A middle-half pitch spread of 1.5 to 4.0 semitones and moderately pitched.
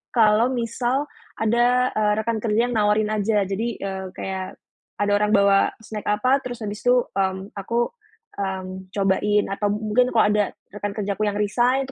No: average, 2.8 semitones; high, 210 Hz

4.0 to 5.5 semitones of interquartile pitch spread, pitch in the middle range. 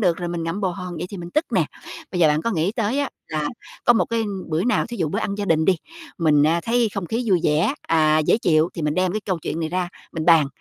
Yes: average, 4.4 semitones; medium, 175 Hz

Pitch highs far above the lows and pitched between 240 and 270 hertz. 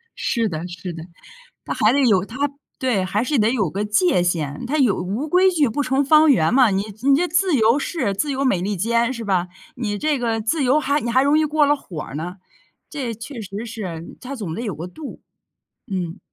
No: wide, 6.6 semitones; high, 230 Hz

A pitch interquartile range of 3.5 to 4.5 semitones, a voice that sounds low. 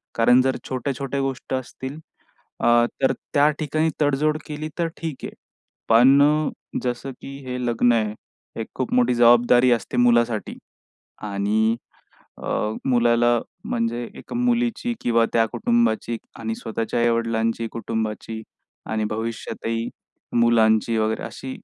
No: average, 3.0 semitones; low, 120 Hz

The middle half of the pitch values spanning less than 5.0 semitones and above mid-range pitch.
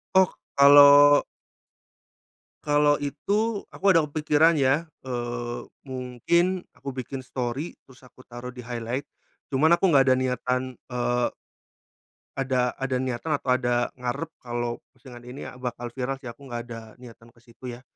No: average, 2.9 semitones; low, 130 Hz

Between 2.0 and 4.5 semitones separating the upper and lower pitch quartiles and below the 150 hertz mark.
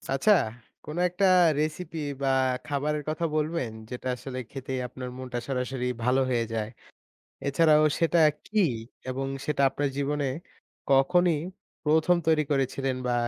Yes: average, 3.2 semitones; medium, 140 Hz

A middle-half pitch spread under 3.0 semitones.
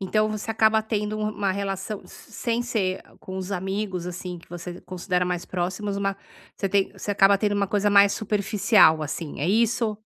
Yes: narrow, 2.5 semitones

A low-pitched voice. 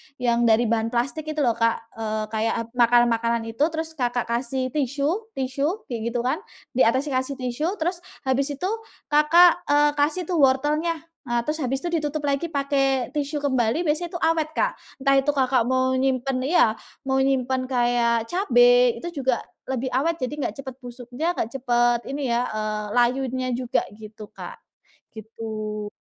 No: very high, 260 Hz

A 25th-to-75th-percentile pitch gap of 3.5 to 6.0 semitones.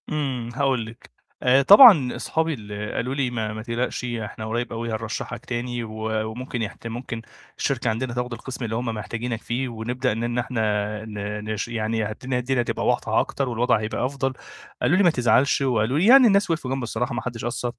No: average, 2.8 semitones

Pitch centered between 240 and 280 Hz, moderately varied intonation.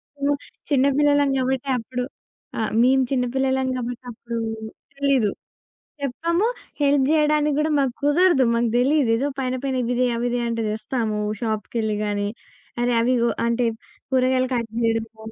Yes: very high, 255 Hz; average, 3.1 semitones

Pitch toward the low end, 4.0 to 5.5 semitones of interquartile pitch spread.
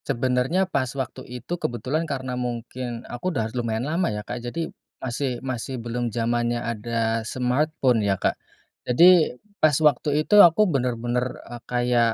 No: low, 125 Hz; average, 3.2 semitones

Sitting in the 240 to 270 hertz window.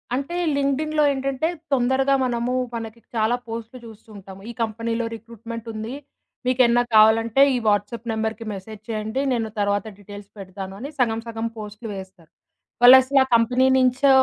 No: high, 230 Hz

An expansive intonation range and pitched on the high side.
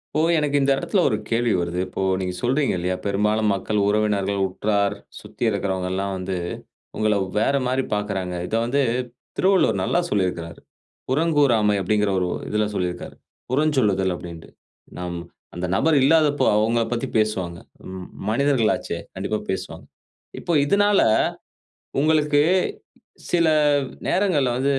No: wide, 6.7 semitones; low, 110 Hz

